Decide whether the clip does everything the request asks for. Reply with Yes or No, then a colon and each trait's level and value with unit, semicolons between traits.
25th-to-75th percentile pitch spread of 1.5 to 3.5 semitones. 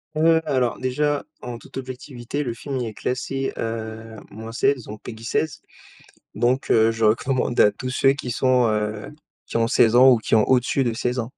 Yes: average, 2.7 semitones